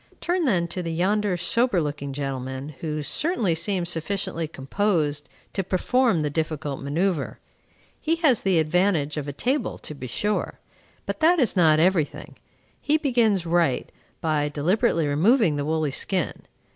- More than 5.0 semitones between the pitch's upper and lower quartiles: Yes, wide, 5.6 semitones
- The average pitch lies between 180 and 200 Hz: No, medium, 170 Hz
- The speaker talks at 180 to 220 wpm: No, average, 150 wpm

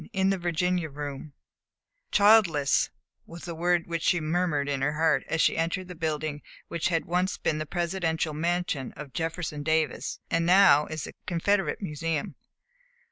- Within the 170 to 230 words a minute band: No, average, 160 wpm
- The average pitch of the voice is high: No, medium, 165 Hz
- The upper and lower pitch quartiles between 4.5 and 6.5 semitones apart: No, average, 2.7 semitones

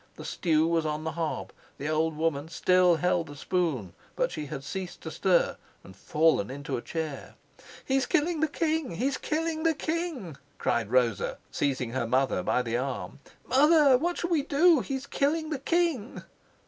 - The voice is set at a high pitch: No, medium, 175 Hz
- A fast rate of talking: No, average, 175 wpm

